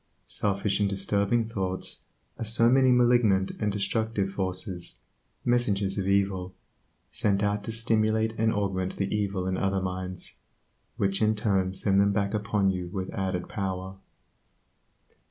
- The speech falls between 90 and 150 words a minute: Yes, average, 140 wpm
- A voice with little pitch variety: Yes, narrow, 2.3 semitones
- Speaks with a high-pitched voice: No, low, 100 Hz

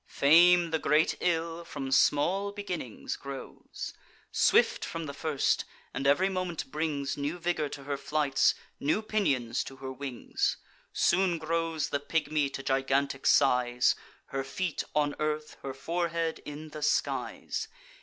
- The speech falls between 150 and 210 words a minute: No, average, 140 wpm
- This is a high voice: No, medium, 150 Hz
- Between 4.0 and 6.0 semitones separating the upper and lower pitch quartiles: No, average, 3.3 semitones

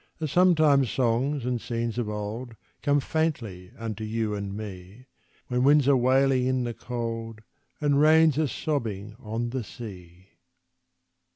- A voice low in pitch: Yes, low, 120 Hz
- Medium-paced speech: Yes, average, 145 wpm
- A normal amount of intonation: Yes, average, 4.4 semitones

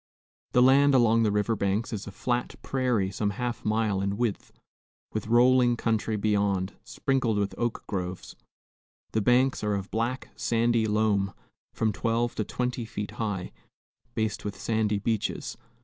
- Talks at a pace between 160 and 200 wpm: No, average, 150 wpm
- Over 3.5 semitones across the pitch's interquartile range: No, average, 2.7 semitones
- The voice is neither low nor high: No, low, 110 Hz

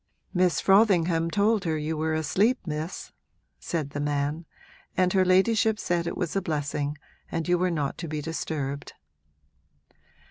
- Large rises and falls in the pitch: No, average, 3.4 semitones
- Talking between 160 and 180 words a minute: No, average, 150 wpm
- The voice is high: No, medium, 165 Hz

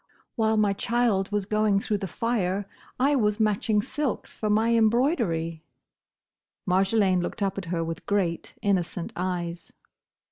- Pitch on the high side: Yes, high, 205 Hz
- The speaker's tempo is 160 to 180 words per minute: No, average, 140 wpm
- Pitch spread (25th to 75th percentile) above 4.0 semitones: No, average, 3.2 semitones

